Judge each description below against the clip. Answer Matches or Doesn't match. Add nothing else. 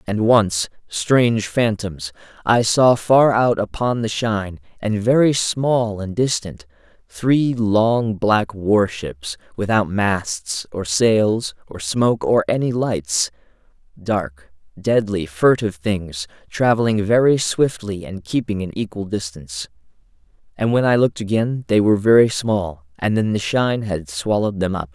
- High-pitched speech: Doesn't match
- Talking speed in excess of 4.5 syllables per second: Doesn't match